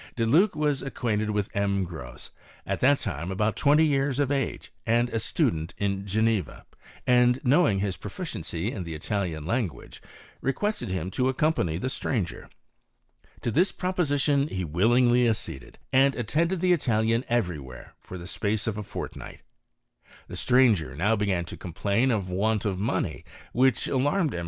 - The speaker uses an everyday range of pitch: No, wide, 5.8 semitones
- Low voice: Yes, low, 110 Hz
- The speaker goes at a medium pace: Yes, average, 155 wpm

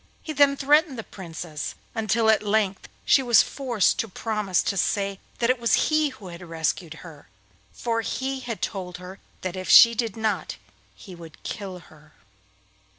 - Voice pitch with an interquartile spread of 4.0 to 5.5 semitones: Yes, average, 4.7 semitones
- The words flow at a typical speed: Yes, average, 165 wpm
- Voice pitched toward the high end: Yes, high, 210 Hz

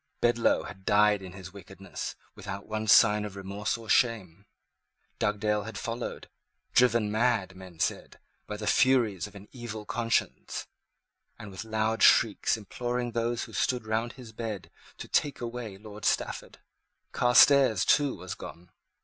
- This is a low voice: Yes, low, 110 Hz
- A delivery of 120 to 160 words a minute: Yes, average, 150 wpm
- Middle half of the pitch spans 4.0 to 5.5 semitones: No, average, 2.9 semitones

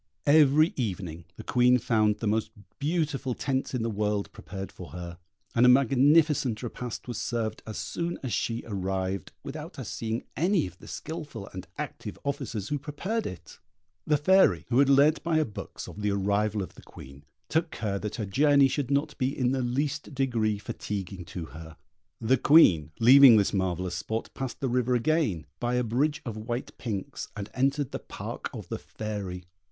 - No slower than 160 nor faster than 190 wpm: Yes, average, 185 wpm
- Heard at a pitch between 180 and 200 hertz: No, low, 120 Hz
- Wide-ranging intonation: Yes, wide, 5.7 semitones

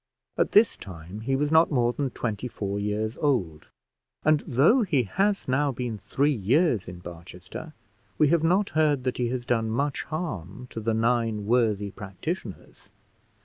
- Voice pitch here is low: Yes, low, 120 Hz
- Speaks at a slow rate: No, average, 165 wpm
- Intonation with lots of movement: Yes, wide, 6.1 semitones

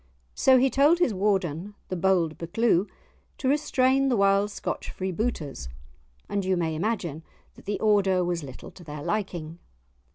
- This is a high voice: Yes, high, 195 Hz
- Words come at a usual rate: Yes, average, 155 wpm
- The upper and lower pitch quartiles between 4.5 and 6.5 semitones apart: Yes, average, 4.9 semitones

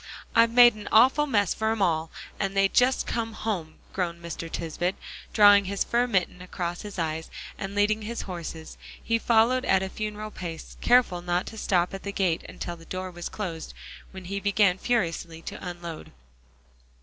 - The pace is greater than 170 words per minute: Yes, average, 180 wpm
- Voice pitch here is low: No, high, 195 Hz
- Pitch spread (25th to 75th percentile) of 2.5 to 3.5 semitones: No, average, 4.0 semitones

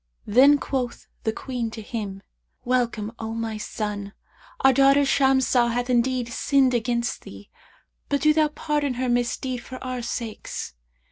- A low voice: No, high, 245 Hz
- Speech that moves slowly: No, average, 145 wpm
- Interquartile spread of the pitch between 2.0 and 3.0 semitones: Yes, narrow, 2.6 semitones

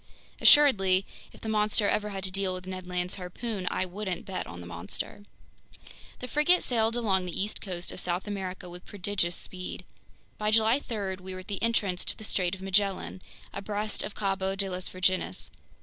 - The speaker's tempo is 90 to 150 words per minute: No, average, 190 wpm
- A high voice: Yes, high, 195 Hz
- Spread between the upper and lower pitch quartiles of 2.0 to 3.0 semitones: Yes, narrow, 2.4 semitones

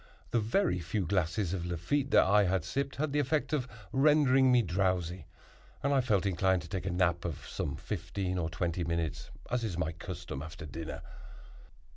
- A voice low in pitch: Yes, very low, 95 Hz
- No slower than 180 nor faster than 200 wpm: Yes, average, 185 wpm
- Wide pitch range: Yes, wide, 6.9 semitones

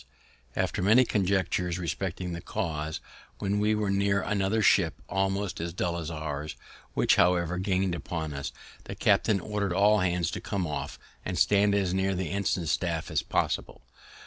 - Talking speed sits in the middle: Yes, average, 165 wpm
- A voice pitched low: Yes, very low, 95 Hz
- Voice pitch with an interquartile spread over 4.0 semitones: No, average, 2.7 semitones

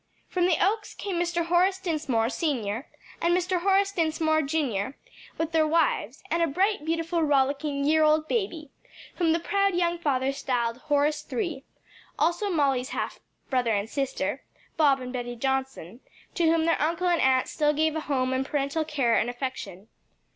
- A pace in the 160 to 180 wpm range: Yes, average, 170 wpm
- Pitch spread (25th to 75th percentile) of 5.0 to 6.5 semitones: No, average, 4.3 semitones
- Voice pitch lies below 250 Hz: No, very high, 305 Hz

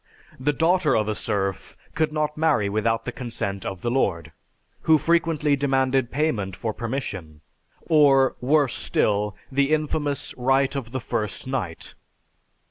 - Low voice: Yes, low, 130 Hz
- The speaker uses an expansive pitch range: Yes, wide, 5.7 semitones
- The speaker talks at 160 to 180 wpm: No, average, 140 wpm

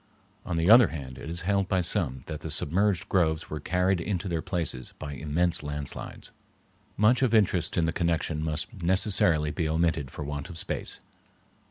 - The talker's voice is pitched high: No, very low, 85 Hz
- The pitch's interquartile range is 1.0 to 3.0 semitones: No, average, 3.4 semitones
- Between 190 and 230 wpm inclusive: No, average, 180 wpm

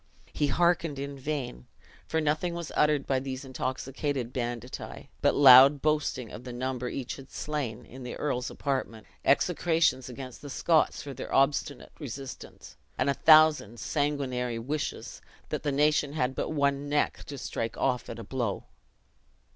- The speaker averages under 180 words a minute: Yes, average, 155 wpm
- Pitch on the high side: No, low, 135 Hz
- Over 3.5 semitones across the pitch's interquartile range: No, average, 2.8 semitones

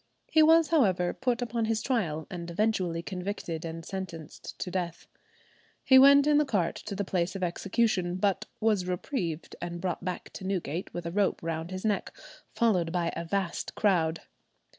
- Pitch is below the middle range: No, medium, 185 Hz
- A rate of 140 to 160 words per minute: No, average, 175 wpm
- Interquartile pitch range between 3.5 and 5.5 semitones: Yes, average, 4.3 semitones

